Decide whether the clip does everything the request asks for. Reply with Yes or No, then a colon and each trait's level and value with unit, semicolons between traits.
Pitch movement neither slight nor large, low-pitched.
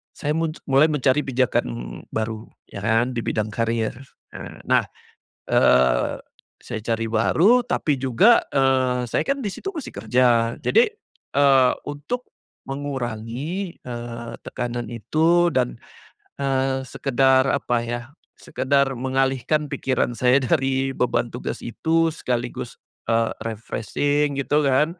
Yes: average, 3.6 semitones; low, 130 Hz